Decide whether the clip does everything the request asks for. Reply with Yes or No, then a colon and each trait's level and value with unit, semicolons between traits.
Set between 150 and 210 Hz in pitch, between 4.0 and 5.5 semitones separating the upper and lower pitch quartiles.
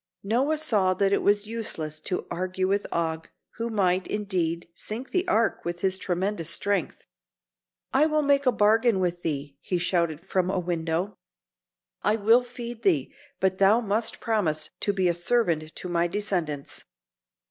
Yes: high, 190 Hz; average, 4.4 semitones